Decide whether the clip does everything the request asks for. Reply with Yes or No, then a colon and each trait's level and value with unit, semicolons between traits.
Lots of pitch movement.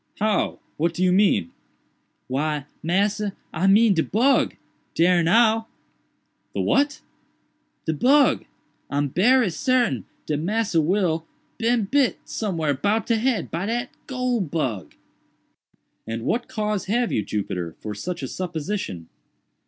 Yes: wide, 6.4 semitones